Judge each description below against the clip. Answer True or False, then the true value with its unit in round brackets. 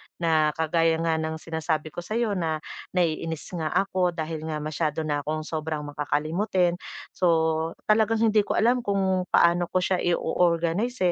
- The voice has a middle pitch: True (165 Hz)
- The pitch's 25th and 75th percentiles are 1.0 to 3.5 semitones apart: True (2.7 semitones)